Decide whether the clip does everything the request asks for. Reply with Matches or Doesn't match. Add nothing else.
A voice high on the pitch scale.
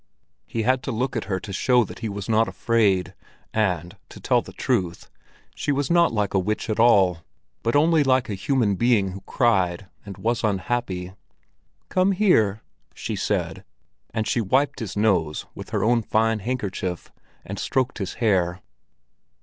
Doesn't match